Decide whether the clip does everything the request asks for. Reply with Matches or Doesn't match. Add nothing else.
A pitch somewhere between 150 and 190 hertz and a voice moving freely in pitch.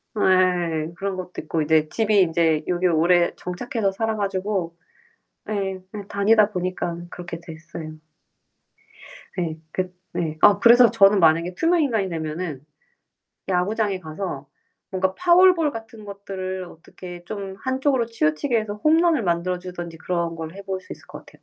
Doesn't match